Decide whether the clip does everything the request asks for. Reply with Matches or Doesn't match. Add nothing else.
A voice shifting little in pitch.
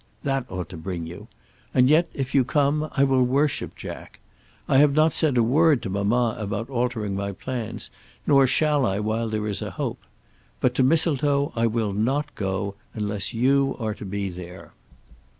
Doesn't match